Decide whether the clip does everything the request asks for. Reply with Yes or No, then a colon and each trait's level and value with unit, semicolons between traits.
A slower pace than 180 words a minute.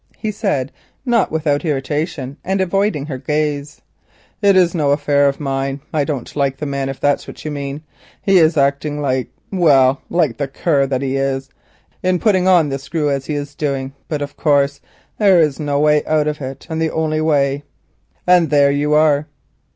No: average, 190 wpm